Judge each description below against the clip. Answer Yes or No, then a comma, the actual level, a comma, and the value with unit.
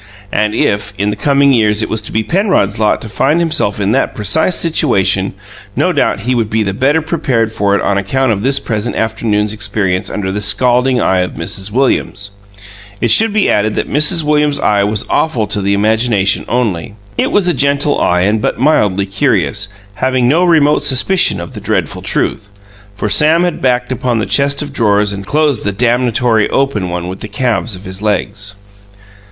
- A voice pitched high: No, low, 110 Hz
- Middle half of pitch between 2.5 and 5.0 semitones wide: No, wide, 5.4 semitones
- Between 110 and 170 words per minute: No, average, 195 wpm